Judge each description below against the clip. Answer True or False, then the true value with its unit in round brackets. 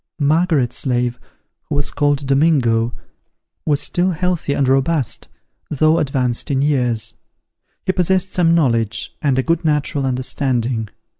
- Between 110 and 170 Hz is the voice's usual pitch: True (140 Hz)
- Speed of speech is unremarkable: False (130 wpm)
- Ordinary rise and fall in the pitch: True (4.2 semitones)